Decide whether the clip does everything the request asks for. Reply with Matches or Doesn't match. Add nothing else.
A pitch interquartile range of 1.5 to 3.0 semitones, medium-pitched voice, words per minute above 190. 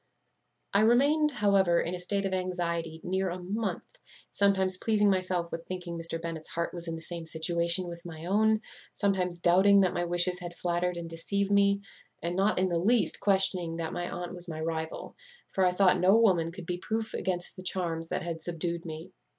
Matches